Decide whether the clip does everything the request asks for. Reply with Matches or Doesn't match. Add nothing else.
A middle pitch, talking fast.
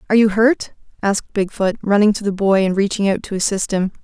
Doesn't match